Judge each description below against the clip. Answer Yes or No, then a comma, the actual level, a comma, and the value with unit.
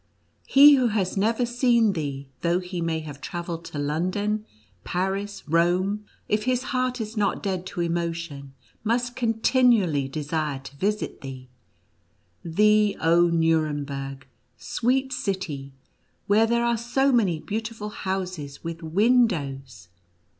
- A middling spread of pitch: No, wide, 6.2 semitones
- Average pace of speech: No, slow, 130 wpm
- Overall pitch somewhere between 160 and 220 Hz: Yes, medium, 185 Hz